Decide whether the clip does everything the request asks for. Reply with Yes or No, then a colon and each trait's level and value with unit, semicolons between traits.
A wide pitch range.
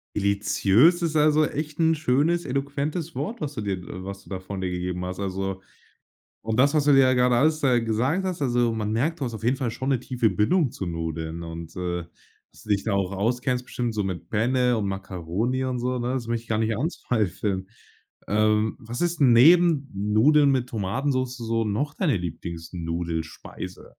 Yes: wide, 6.0 semitones